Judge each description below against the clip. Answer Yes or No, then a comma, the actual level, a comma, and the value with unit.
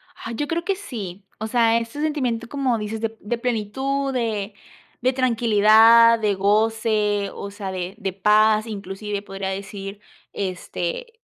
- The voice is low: No, high, 220 Hz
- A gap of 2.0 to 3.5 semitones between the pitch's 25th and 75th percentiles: Yes, average, 2.9 semitones